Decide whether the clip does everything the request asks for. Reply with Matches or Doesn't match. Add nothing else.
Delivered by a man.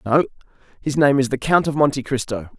Matches